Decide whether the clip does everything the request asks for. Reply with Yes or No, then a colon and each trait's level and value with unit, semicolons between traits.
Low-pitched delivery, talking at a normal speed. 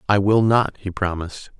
Yes: low, 100 Hz; average, 190 wpm